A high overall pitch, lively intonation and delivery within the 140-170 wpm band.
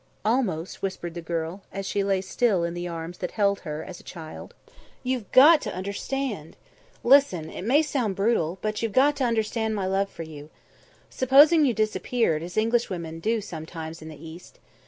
No: high, 195 Hz; wide, 5.8 semitones; average, 180 wpm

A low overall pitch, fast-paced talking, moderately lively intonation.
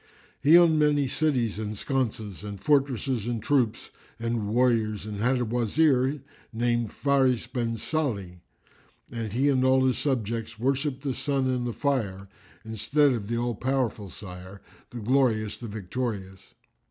No: low, 120 Hz; average, 150 wpm; average, 3.9 semitones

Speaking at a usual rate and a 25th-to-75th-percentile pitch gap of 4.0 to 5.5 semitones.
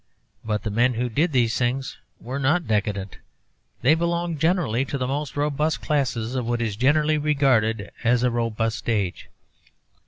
Yes: average, 160 wpm; average, 4.7 semitones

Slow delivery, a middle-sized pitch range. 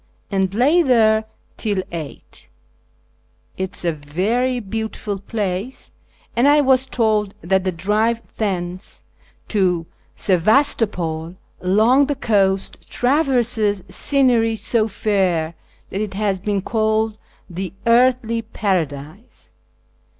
Yes: slow, 110 wpm; average, 3.8 semitones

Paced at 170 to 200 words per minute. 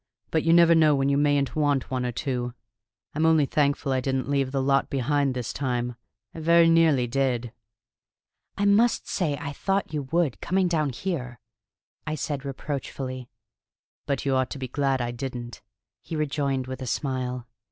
Yes: average, 175 wpm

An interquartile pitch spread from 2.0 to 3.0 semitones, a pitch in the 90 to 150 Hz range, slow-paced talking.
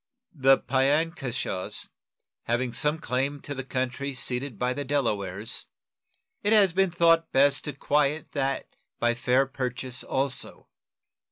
Yes: narrow, 2.6 semitones; low, 135 Hz; slow, 125 wpm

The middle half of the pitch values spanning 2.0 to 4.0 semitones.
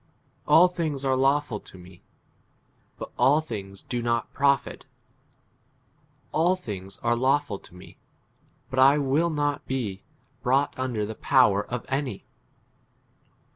No: wide, 5.4 semitones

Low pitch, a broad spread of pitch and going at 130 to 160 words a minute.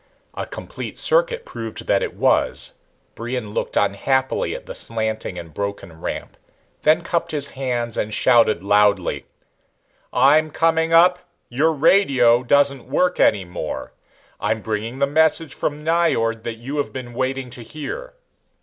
Yes: low, 130 Hz; wide, 6.0 semitones; average, 145 wpm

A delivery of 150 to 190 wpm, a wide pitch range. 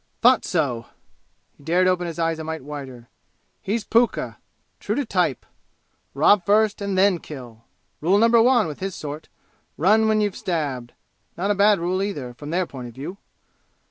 Yes: average, 175 wpm; wide, 5.7 semitones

